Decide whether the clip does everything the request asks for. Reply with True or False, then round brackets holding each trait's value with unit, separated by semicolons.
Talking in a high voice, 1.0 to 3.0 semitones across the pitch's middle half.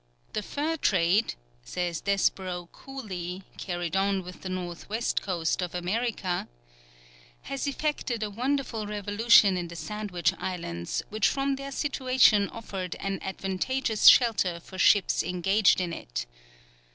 False (195 Hz; 4.4 semitones)